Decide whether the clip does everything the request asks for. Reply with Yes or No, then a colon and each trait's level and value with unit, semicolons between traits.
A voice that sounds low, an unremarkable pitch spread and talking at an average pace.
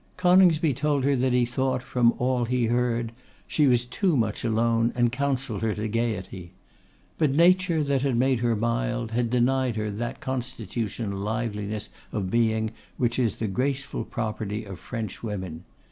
Yes: low, 120 Hz; average, 3.1 semitones; average, 160 wpm